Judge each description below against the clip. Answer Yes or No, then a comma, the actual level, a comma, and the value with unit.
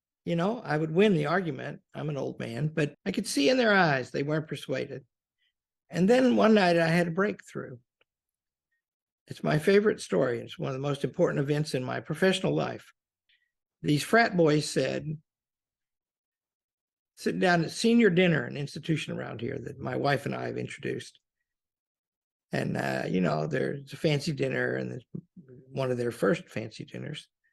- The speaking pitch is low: No, medium, 160 Hz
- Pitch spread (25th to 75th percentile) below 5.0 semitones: No, wide, 5.6 semitones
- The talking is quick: No, average, 170 wpm